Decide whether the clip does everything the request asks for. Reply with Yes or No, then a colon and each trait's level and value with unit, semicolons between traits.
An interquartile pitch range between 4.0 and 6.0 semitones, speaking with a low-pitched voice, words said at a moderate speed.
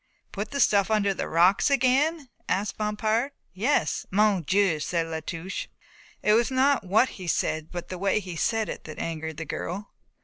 No: average, 4.6 semitones; high, 200 Hz; average, 180 wpm